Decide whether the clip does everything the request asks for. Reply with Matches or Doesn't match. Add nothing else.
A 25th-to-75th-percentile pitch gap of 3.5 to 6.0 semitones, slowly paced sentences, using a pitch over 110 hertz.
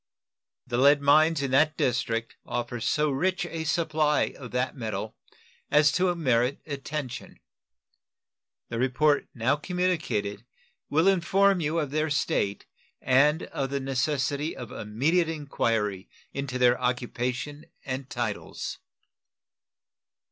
Matches